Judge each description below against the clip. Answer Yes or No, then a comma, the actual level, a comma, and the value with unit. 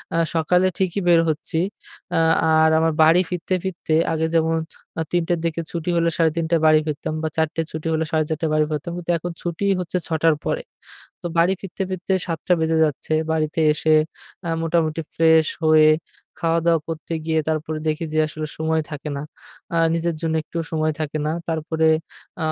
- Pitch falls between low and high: Yes, medium, 160 Hz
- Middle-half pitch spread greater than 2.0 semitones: No, narrow, 1.3 semitones